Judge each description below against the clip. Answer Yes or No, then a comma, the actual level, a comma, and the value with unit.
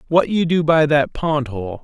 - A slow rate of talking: No, fast, 230 wpm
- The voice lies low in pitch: No, medium, 150 Hz